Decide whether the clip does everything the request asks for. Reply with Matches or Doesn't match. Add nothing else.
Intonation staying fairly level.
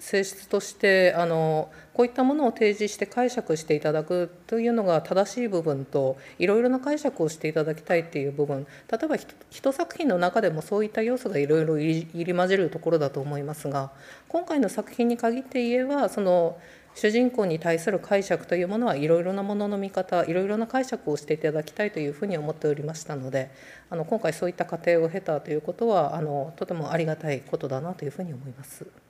Doesn't match